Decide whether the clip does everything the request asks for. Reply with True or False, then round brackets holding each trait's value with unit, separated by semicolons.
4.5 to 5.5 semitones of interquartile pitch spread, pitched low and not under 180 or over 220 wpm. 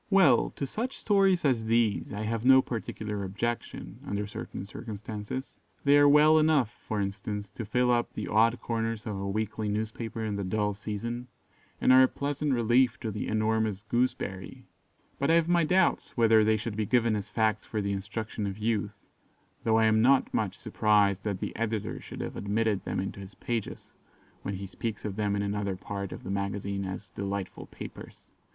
False (2.9 semitones; 110 Hz; 190 wpm)